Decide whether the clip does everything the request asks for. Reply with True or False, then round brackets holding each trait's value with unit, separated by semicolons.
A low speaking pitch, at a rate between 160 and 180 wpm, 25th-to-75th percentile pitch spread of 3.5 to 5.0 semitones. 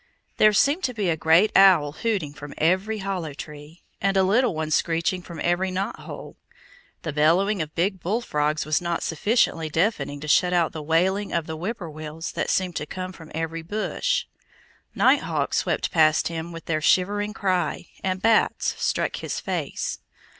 False (175 Hz; 170 wpm; 3.8 semitones)